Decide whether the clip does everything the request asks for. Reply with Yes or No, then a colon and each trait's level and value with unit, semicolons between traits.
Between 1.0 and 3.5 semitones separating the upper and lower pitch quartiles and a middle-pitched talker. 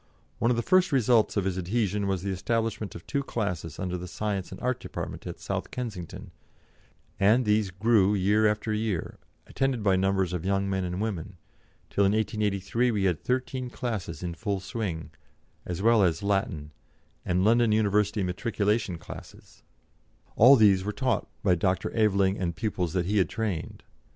No: average, 3.2 semitones; low, 100 Hz